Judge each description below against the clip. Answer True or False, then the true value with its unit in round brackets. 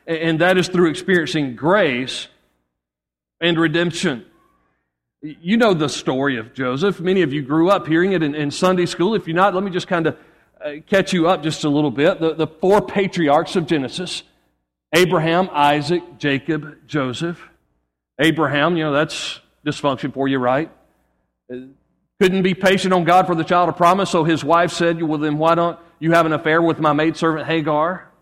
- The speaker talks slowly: False (175 wpm)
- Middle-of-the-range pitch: True (160 Hz)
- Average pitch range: True (3.4 semitones)